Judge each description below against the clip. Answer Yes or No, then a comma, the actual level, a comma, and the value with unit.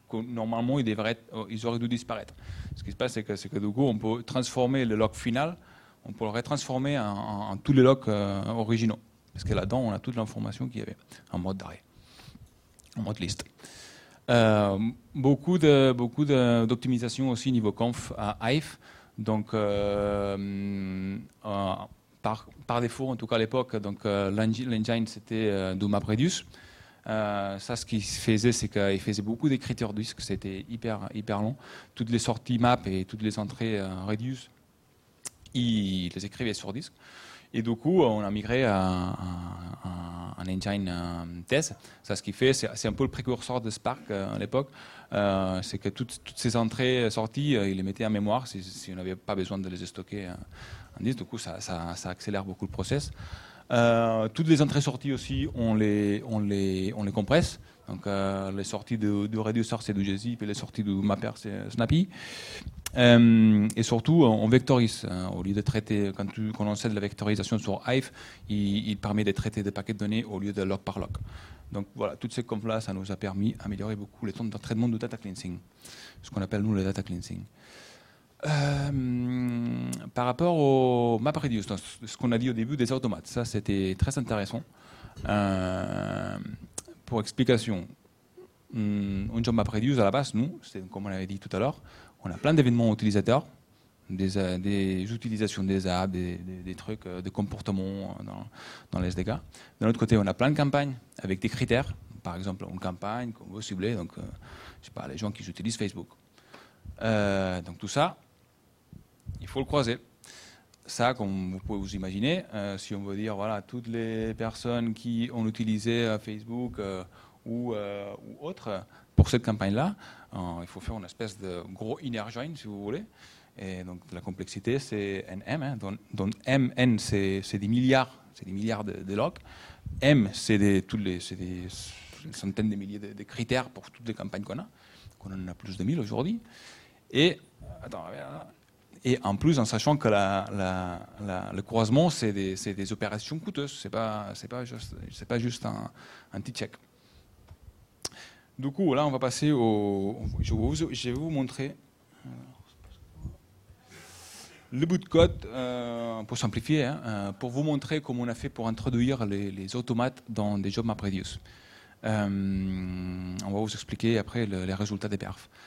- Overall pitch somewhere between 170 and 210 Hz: No, low, 110 Hz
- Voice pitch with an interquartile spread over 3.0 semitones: Yes, average, 3.5 semitones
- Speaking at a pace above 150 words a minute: Yes, average, 185 wpm